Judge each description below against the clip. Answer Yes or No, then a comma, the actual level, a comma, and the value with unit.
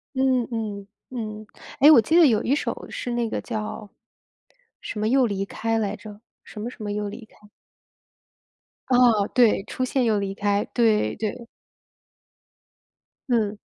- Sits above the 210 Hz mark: Yes, high, 220 Hz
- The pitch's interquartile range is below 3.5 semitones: Yes, average, 2.8 semitones